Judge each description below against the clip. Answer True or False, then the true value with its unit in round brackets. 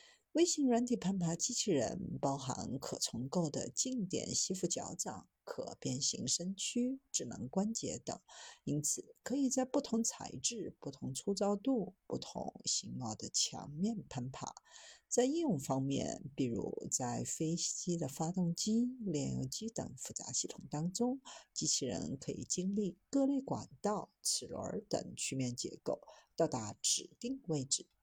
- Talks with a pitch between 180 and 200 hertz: True (190 Hz)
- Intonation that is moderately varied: False (7.7 semitones)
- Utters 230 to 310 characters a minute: False (220 characters per minute)